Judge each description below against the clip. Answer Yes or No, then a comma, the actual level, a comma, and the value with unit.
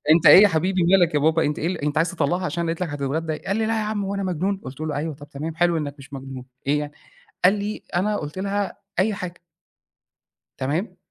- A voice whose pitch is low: No, medium, 170 Hz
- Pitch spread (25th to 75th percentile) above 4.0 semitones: Yes, average, 4.5 semitones